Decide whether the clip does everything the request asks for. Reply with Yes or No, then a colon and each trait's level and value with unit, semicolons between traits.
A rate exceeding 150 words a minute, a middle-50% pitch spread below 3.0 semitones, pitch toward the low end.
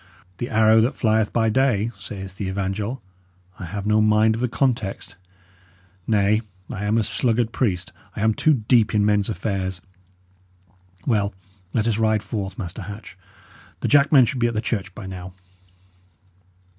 Yes: average, 160 wpm; narrow, 2.4 semitones; low, 110 Hz